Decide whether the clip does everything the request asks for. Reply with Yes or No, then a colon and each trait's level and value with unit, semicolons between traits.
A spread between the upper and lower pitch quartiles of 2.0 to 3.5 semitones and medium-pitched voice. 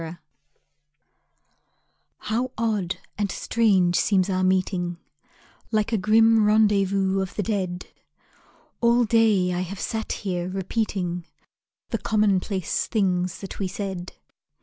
No: average, 2.9 semitones; high, 195 Hz